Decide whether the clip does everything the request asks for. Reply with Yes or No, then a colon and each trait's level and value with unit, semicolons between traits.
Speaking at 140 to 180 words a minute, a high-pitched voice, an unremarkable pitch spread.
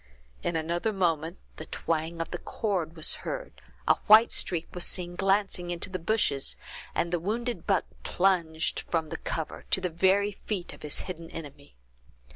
No: average, 170 wpm; medium, 175 Hz; average, 3.0 semitones